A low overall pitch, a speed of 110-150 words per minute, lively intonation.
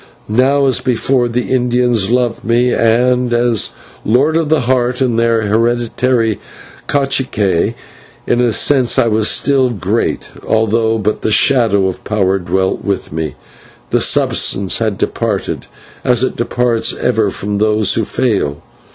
No: low, 115 Hz; average, 140 wpm; average, 2.7 semitones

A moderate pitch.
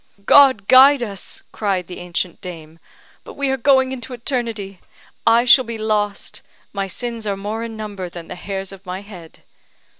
No: high, 210 Hz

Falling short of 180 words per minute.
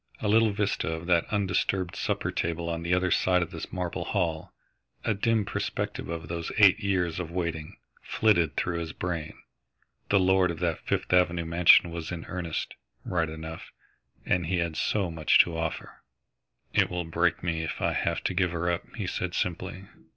No: average, 185 wpm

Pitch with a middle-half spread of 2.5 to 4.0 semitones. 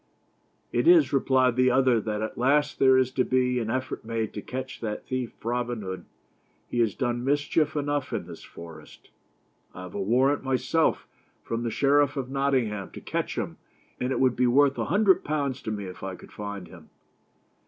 Yes: average, 3.7 semitones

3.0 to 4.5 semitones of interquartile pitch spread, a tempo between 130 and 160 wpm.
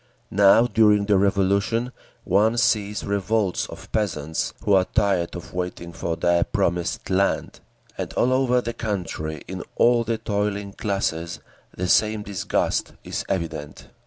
Yes: average, 3.5 semitones; average, 140 wpm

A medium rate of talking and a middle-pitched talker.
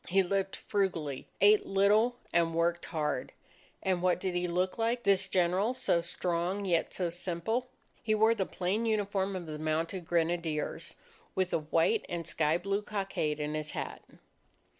Yes: average, 160 wpm; medium, 180 Hz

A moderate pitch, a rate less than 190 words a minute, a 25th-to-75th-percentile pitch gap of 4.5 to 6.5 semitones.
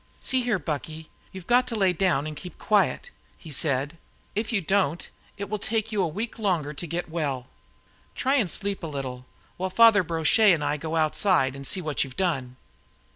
No: medium, 170 Hz; average, 195 wpm; wide, 5.4 semitones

